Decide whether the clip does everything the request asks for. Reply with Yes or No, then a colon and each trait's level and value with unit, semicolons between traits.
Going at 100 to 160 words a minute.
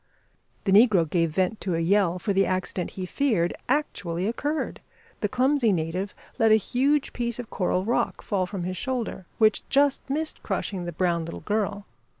No: average, 175 wpm